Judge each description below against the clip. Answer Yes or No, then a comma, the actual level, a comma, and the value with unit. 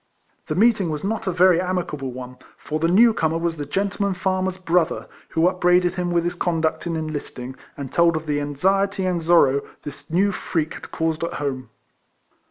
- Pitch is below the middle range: No, medium, 170 Hz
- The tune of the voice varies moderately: Yes, average, 3.2 semitones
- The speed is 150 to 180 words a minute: No, average, 190 wpm